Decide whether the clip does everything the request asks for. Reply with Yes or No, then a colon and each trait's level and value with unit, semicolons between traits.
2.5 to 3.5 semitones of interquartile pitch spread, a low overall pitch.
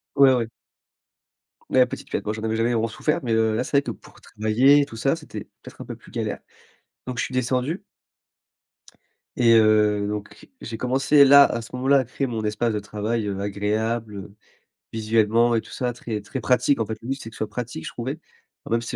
Yes: average, 2.9 semitones; low, 115 Hz